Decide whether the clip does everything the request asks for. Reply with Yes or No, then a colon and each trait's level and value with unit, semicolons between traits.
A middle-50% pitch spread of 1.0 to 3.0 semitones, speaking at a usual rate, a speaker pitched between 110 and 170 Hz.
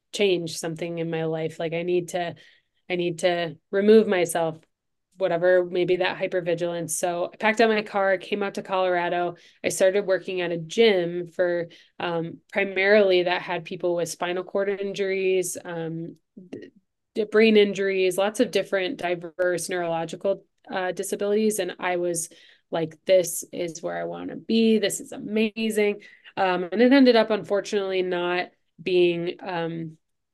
No: narrow, 2.5 semitones; average, 150 wpm; medium, 185 Hz